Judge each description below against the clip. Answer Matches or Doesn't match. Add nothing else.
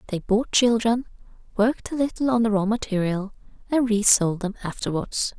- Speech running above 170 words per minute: Doesn't match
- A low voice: Doesn't match